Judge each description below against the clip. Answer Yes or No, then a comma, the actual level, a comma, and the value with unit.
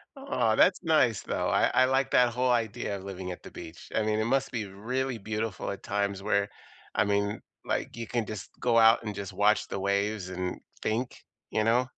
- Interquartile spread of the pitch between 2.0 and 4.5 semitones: Yes, average, 3.3 semitones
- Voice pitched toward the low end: Yes, low, 110 Hz